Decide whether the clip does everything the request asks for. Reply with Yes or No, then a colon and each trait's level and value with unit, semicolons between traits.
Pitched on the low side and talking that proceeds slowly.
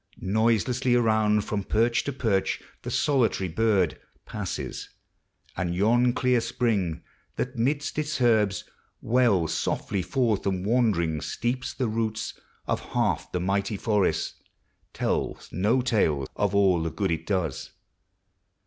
Yes: low, 110 Hz; slow, 130 wpm